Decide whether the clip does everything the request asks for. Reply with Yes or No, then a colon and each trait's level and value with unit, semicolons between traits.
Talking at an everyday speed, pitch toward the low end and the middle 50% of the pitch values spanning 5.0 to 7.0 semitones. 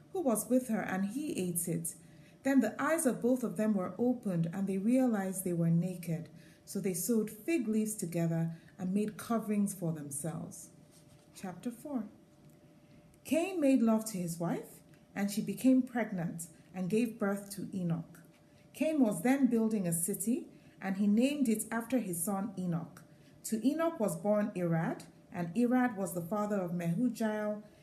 No: average, 165 wpm; high, 200 Hz; average, 5.3 semitones